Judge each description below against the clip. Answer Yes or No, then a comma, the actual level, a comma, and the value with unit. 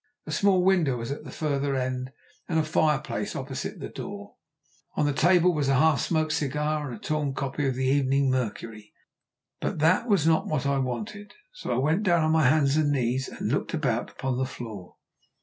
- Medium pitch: Yes, medium, 145 Hz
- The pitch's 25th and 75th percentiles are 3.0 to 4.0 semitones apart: Yes, average, 3.3 semitones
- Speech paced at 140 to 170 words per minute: No, average, 200 wpm